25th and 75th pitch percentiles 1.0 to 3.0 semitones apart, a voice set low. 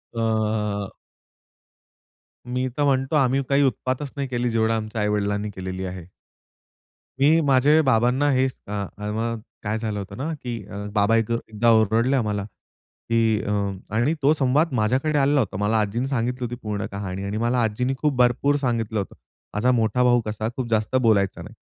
No: average, 3.7 semitones; low, 115 Hz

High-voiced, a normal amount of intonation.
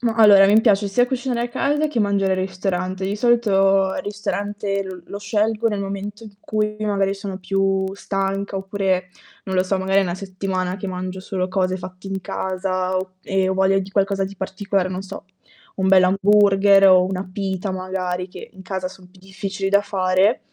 No: high, 195 Hz; narrow, 1.4 semitones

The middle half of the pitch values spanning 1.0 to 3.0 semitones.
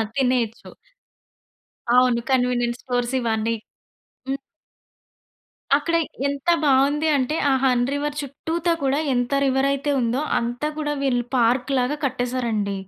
Yes: narrow, 2.5 semitones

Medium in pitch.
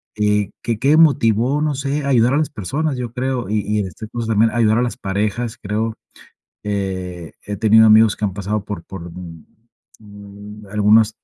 No: low, 110 Hz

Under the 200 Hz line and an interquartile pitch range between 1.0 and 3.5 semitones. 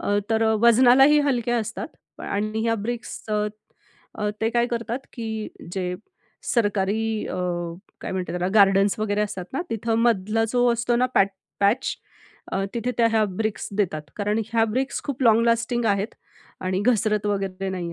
No: high, 220 Hz; average, 2.7 semitones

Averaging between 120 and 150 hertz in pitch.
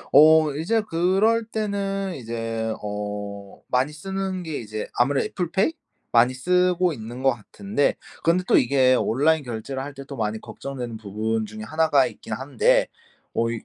Yes: medium, 140 Hz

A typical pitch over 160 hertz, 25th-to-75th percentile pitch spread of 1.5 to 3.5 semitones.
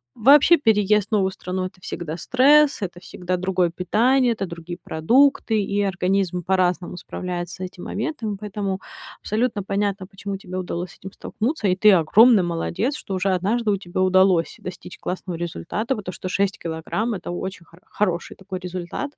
Yes: high, 190 Hz; average, 2.9 semitones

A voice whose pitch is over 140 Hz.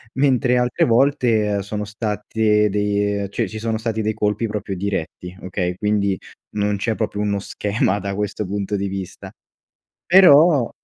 No: low, 105 Hz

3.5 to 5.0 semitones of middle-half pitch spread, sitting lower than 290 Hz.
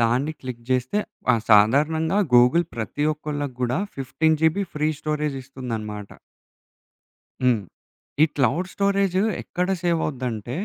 Yes: average, 4.7 semitones; medium, 140 Hz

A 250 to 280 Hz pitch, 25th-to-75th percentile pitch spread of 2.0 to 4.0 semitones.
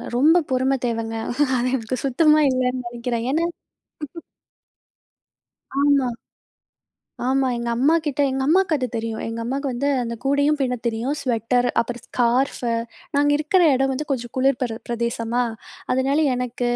Yes: very high, 255 Hz; average, 2.9 semitones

